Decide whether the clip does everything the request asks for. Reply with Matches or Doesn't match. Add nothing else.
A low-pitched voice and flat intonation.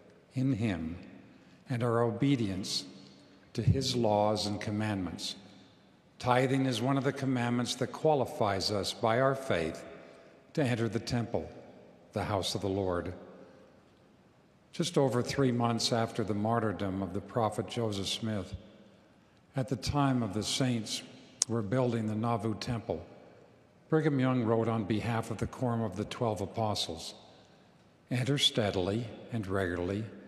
Doesn't match